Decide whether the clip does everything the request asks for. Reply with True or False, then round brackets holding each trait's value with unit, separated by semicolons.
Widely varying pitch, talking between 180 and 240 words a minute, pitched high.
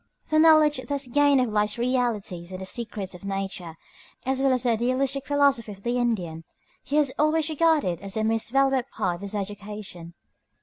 True (5.7 semitones; 190 wpm; 235 Hz)